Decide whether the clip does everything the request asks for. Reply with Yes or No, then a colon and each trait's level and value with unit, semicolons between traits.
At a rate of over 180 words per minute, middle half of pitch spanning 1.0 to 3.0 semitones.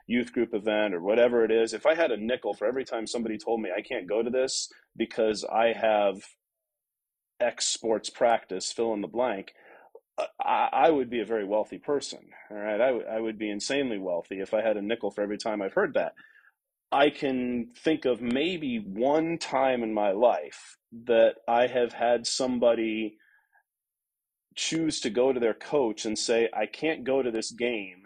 No: average, 195 wpm; average, 3.4 semitones